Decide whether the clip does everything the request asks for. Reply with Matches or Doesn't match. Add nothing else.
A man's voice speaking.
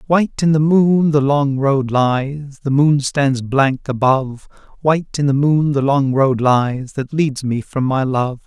Matches